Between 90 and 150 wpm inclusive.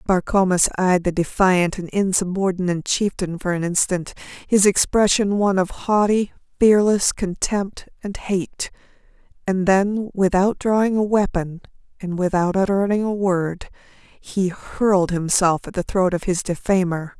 Yes: average, 140 wpm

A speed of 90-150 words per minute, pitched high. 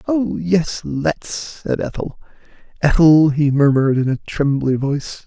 No: slow, 135 wpm; medium, 140 Hz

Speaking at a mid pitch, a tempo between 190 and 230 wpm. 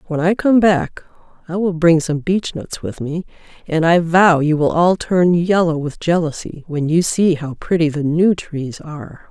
Yes: medium, 165 Hz; average, 200 wpm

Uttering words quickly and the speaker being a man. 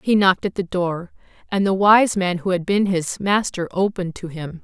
No: fast, 220 wpm; female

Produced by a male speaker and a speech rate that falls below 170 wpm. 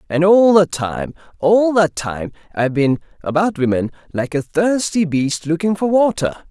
Yes: male; average, 150 wpm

